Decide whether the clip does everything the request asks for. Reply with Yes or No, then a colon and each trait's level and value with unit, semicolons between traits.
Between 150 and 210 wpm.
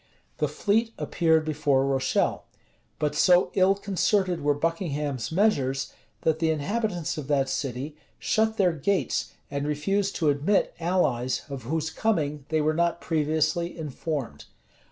No: slow, 135 wpm